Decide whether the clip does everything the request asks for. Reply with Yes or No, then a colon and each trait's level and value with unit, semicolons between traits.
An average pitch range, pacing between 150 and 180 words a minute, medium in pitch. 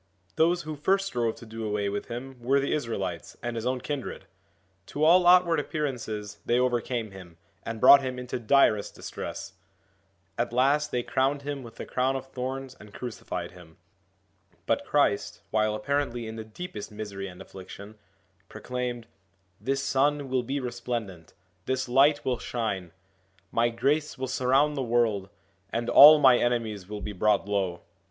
No: average, 4.2 semitones; average, 165 wpm; low, 120 Hz